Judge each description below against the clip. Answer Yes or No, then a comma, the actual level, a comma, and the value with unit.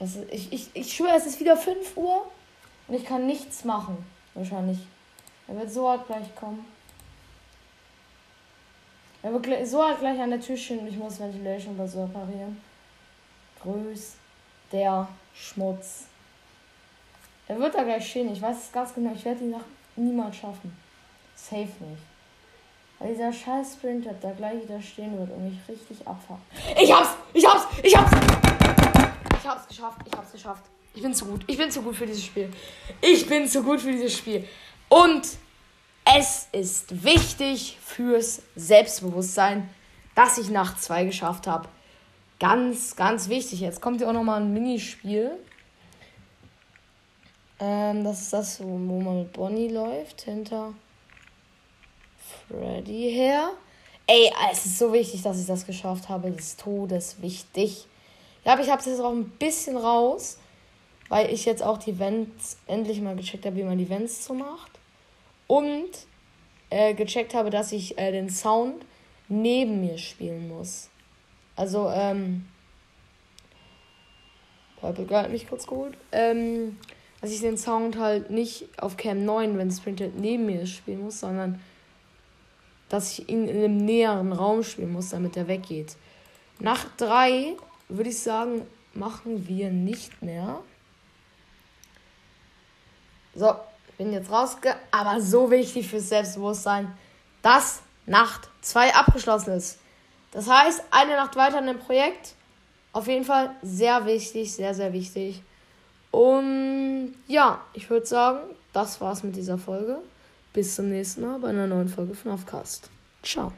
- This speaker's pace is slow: No, average, 150 wpm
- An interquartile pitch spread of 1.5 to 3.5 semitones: No, average, 4.1 semitones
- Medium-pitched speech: No, high, 215 Hz